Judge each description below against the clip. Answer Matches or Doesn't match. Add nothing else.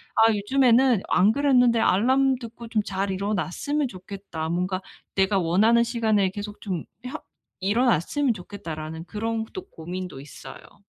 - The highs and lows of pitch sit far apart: Doesn't match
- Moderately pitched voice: Doesn't match